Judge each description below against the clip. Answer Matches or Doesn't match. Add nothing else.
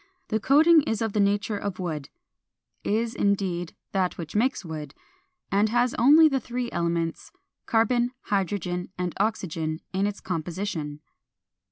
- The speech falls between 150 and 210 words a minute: Doesn't match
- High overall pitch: Matches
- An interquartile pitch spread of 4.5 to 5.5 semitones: Matches